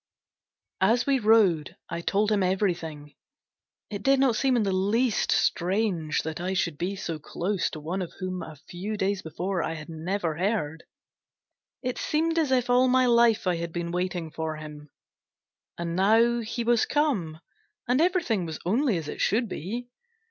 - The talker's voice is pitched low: No, high, 190 Hz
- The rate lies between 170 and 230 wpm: Yes, average, 175 wpm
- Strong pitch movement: Yes, wide, 5.8 semitones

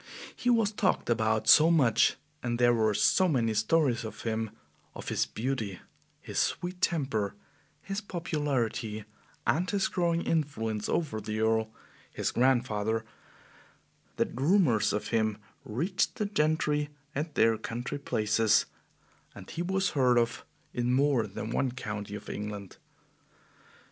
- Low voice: Yes, low, 120 Hz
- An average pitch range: No, wide, 6.2 semitones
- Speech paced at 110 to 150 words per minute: Yes, slow, 135 wpm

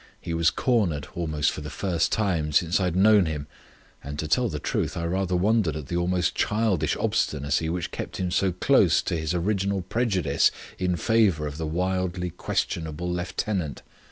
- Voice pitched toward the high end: No, very low, 90 Hz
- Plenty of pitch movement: No, average, 3.3 semitones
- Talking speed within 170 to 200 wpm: Yes, average, 180 wpm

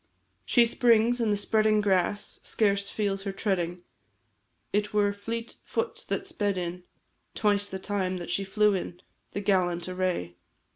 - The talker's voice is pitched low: No, high, 200 Hz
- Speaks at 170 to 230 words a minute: No, average, 150 wpm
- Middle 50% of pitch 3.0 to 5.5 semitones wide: No, narrow, 2.5 semitones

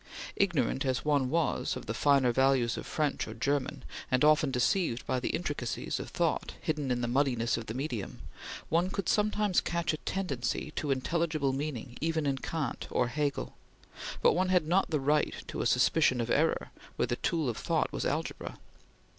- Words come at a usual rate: Yes, average, 185 wpm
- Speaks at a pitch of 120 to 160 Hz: Yes, medium, 140 Hz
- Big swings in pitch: No, average, 4.3 semitones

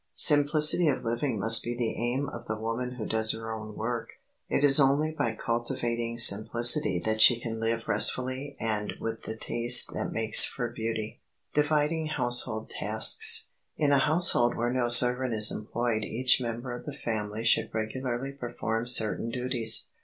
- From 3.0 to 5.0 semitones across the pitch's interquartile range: No, narrow, 2.6 semitones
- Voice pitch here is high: No, low, 120 Hz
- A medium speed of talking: Yes, average, 170 wpm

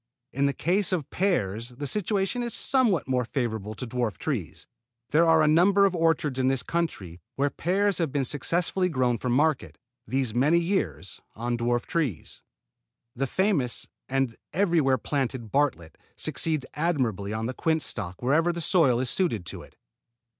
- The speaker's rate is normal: Yes, average, 165 wpm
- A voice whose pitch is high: No, medium, 140 Hz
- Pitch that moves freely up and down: Yes, wide, 6.0 semitones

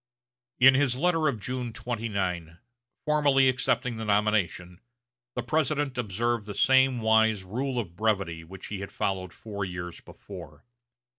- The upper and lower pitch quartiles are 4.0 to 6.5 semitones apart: Yes, average, 5.1 semitones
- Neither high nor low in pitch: No, low, 110 Hz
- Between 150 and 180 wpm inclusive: No, average, 140 wpm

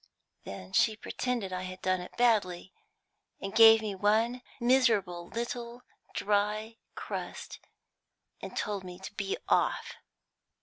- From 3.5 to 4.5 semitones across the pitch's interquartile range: Yes, average, 3.8 semitones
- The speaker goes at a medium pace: No, slow, 125 wpm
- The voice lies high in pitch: Yes, high, 210 Hz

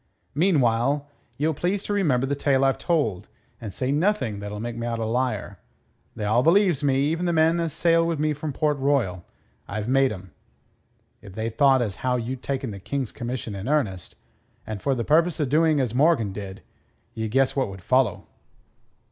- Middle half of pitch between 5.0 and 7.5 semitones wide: Yes, average, 5.3 semitones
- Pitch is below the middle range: Yes, low, 130 Hz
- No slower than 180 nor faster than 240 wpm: Yes, average, 190 wpm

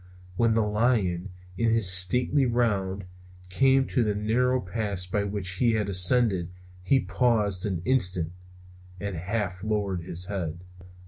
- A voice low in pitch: Yes, low, 105 Hz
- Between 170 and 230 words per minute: No, average, 140 wpm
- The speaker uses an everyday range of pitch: Yes, average, 4.0 semitones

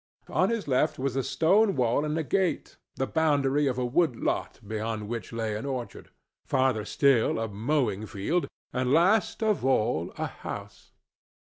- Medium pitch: No, low, 130 Hz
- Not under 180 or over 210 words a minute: No, average, 165 wpm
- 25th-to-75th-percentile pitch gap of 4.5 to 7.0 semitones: Yes, wide, 5.4 semitones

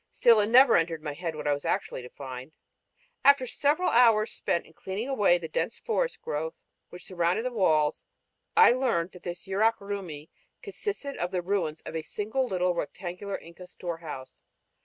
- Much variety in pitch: Yes, wide, 5.8 semitones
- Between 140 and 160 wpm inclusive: No, average, 180 wpm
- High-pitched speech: No, medium, 180 Hz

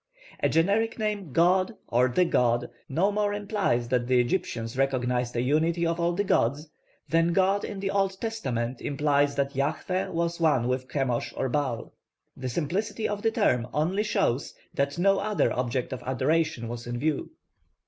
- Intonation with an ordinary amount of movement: No, wide, 7.1 semitones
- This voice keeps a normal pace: Yes, average, 170 wpm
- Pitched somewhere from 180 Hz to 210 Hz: No, medium, 150 Hz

